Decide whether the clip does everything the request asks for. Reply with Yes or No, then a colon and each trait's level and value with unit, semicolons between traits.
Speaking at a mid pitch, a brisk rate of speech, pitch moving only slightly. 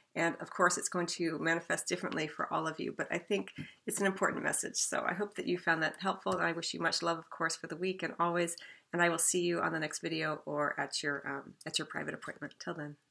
Yes: medium, 165 Hz; fast, 270 wpm; narrow, 2.2 semitones